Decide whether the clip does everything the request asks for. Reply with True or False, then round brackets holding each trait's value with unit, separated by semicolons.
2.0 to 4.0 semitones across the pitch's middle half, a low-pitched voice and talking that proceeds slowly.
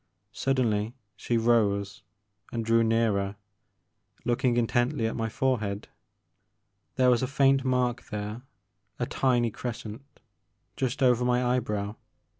True (2.7 semitones; 120 Hz; 115 wpm)